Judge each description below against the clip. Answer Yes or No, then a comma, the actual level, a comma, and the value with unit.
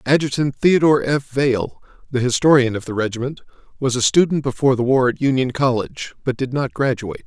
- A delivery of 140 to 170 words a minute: No, average, 180 wpm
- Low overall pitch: Yes, low, 130 Hz